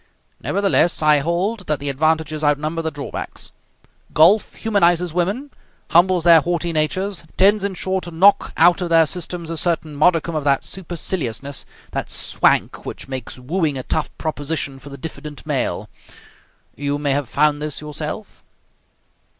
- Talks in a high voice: No, medium, 160 Hz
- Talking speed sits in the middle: Yes, average, 150 wpm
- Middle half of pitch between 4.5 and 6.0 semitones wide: No, average, 3.3 semitones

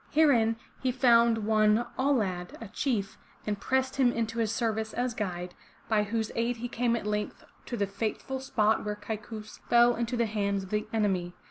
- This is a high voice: Yes, high, 225 Hz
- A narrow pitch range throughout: Yes, narrow, 2.3 semitones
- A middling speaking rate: Yes, average, 190 wpm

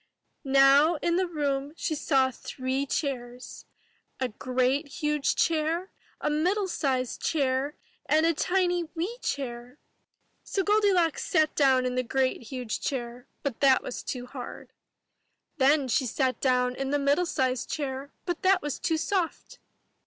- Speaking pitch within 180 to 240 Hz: No, very high, 280 Hz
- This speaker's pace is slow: No, average, 150 wpm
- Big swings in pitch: No, average, 4.2 semitones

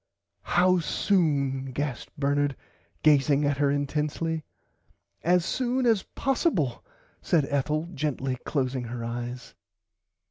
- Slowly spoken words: Yes, slow, 105 wpm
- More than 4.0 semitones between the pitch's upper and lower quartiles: No, average, 3.6 semitones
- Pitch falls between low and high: Yes, medium, 145 Hz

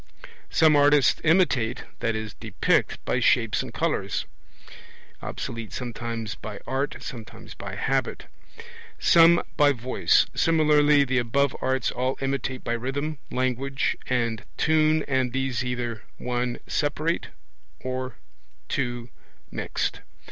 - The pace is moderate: No, slow, 110 wpm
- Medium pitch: No, low, 130 Hz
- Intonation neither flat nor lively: Yes, average, 3.2 semitones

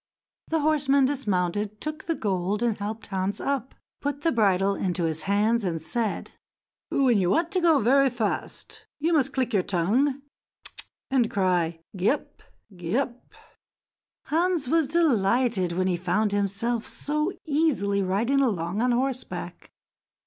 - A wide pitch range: Yes, wide, 6.3 semitones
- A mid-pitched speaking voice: No, high, 230 Hz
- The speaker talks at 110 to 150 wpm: Yes, average, 145 wpm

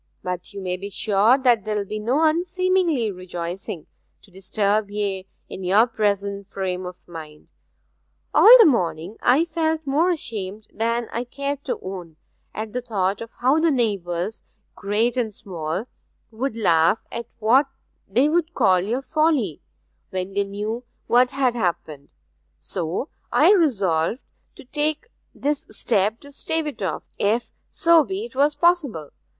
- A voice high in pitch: Yes, high, 220 Hz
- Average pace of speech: Yes, average, 150 wpm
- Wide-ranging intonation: Yes, wide, 6.7 semitones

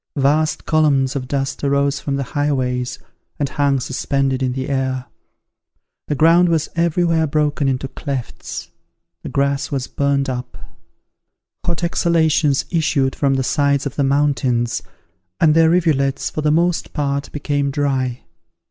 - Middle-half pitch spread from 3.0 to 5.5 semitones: No, narrow, 2.4 semitones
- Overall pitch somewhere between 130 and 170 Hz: Yes, medium, 140 Hz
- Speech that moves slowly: No, average, 145 wpm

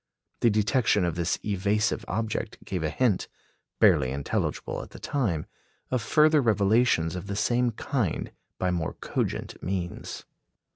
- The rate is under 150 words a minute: Yes, average, 140 wpm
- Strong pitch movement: No, average, 4.9 semitones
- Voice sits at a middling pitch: No, low, 105 Hz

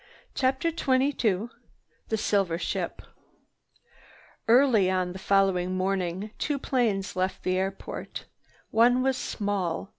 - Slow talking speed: Yes, slow, 110 wpm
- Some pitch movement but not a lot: Yes, average, 5.0 semitones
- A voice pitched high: Yes, high, 200 Hz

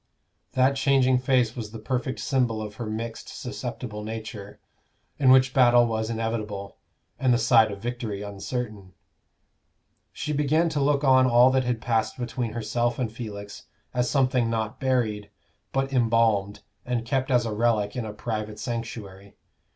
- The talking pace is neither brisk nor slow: Yes, average, 155 wpm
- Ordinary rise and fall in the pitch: Yes, average, 3.0 semitones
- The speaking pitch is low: Yes, low, 120 Hz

